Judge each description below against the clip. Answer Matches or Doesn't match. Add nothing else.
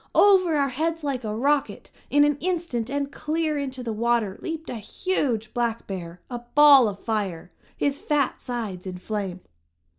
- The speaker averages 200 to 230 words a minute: Doesn't match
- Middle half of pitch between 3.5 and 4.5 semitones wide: Doesn't match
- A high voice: Matches